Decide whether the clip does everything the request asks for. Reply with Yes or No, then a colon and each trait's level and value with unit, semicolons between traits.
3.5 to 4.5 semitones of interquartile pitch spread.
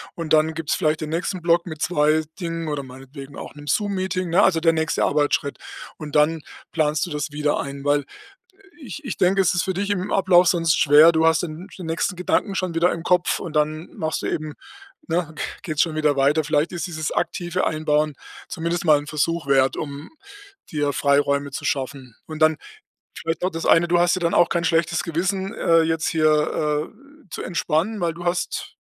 No: narrow, 2.6 semitones